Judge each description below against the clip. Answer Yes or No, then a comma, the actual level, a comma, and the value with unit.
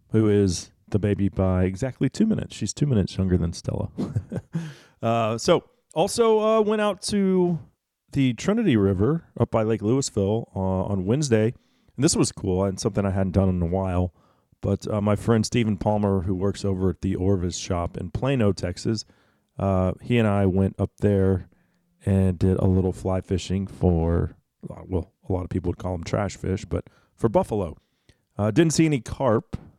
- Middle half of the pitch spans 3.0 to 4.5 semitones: Yes, average, 4.0 semitones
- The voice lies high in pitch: No, low, 100 Hz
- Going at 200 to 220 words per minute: No, average, 185 wpm